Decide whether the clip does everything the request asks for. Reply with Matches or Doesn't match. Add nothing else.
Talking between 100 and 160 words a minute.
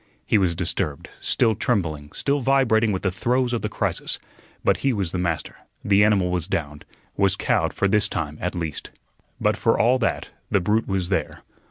Doesn't match